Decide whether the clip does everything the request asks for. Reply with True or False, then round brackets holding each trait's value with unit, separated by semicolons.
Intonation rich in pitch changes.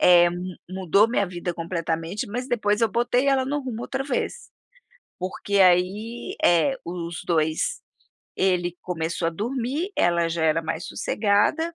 True (5.8 semitones)